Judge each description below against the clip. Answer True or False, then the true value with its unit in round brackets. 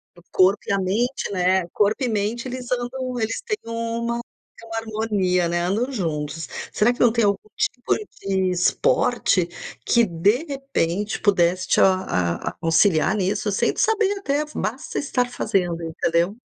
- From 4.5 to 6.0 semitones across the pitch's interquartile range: True (5.0 semitones)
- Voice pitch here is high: True (210 Hz)